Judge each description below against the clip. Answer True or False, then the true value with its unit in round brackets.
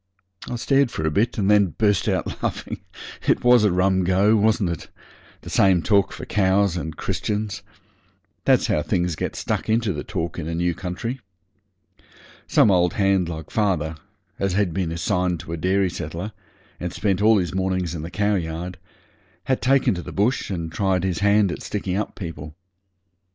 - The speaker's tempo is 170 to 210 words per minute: True (180 wpm)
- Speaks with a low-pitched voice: True (95 Hz)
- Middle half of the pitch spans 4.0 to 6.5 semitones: False (3.2 semitones)